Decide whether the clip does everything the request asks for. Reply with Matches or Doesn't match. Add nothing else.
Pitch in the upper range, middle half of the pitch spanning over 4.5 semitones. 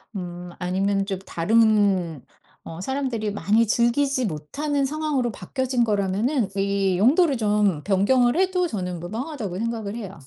Matches